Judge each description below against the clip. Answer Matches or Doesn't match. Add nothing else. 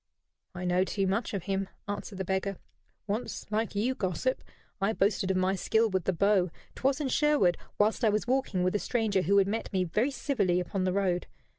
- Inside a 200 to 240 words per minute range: Matches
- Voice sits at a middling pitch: Doesn't match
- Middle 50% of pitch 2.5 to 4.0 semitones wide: Matches